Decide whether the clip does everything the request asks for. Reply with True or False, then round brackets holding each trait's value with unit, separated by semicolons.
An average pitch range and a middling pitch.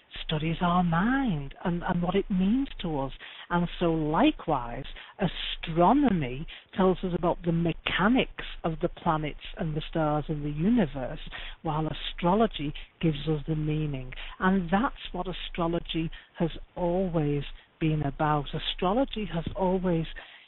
True (3.2 semitones; 170 Hz)